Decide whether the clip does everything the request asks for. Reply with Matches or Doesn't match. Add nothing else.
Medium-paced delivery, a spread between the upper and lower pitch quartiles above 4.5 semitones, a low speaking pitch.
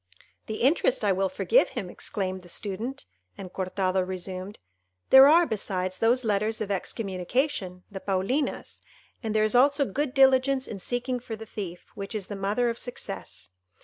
Doesn't match